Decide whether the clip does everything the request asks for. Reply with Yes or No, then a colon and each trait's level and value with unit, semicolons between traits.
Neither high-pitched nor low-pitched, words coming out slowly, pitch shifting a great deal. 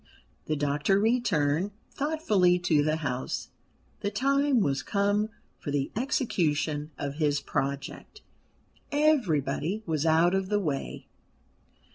Yes: medium, 175 Hz; slow, 115 wpm; wide, 6.3 semitones